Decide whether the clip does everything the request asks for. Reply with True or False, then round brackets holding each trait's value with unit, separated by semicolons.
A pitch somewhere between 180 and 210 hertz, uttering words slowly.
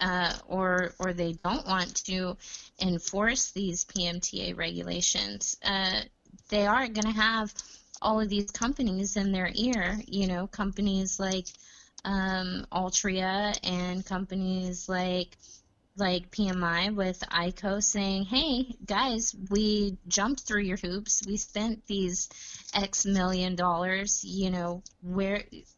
True (190 Hz; 130 wpm)